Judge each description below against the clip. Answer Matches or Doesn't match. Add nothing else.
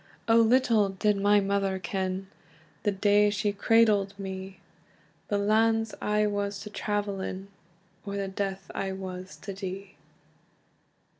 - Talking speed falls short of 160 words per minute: Matches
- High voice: Matches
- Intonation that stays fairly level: Matches